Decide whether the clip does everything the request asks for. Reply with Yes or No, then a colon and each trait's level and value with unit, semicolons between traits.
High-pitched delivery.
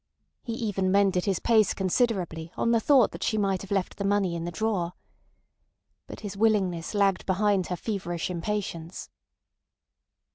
Yes: high, 195 Hz